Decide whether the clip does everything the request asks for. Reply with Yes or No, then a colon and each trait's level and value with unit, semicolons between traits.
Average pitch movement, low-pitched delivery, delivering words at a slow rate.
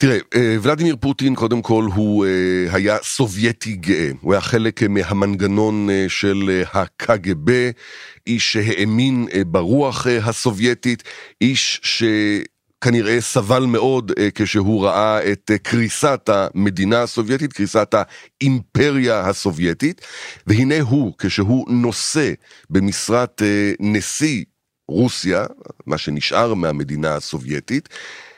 Yes: average, 3.6 semitones; low, 110 Hz; slow, 90 wpm